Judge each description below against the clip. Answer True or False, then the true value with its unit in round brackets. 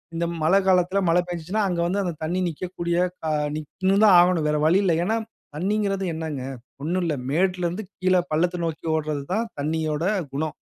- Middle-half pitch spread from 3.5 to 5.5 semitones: False (2.8 semitones)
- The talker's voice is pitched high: False (175 Hz)